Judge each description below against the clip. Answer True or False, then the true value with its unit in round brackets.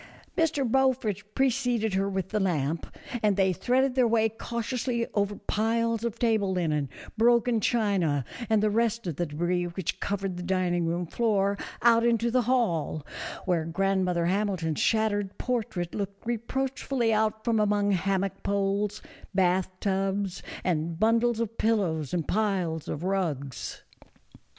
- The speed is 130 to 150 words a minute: True (140 wpm)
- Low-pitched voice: False (200 Hz)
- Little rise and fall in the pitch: False (4.3 semitones)